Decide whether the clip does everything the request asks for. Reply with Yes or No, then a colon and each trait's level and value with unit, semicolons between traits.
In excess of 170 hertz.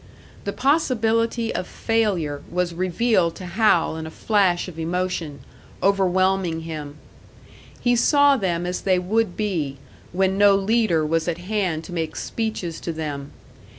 Yes: medium, 185 Hz